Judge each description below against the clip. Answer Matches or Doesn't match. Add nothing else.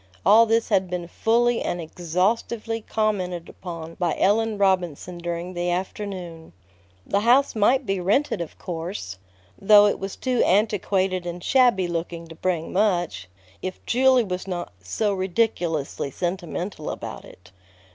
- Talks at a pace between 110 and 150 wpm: Matches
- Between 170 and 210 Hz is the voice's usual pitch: Matches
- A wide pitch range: Doesn't match